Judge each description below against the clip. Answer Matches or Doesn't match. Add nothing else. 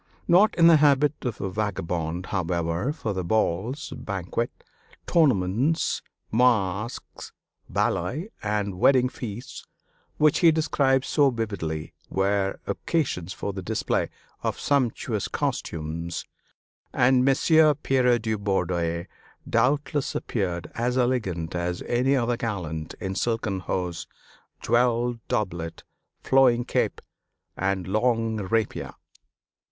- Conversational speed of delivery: Doesn't match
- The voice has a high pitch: Doesn't match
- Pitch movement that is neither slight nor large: Doesn't match